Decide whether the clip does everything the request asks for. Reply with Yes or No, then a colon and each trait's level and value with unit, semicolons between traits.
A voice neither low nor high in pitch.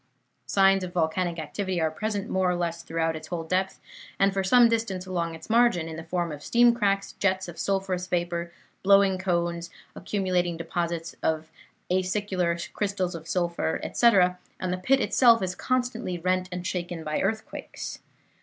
Yes: medium, 180 Hz